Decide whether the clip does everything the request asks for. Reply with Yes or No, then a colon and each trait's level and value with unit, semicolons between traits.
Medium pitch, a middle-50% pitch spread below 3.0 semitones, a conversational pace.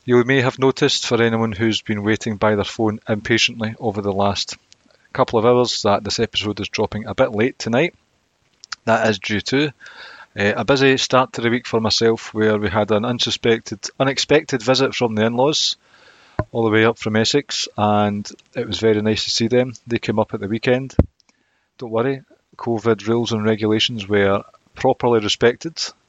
No: low, 115 Hz; narrow, 2.5 semitones; average, 185 wpm